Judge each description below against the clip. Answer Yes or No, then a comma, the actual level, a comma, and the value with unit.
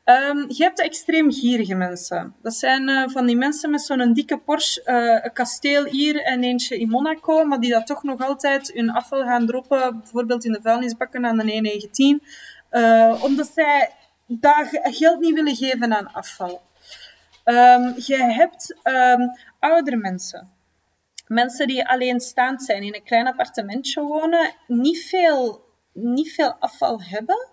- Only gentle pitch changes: No, average, 4.0 semitones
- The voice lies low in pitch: No, very high, 255 Hz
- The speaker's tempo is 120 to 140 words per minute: No, average, 160 wpm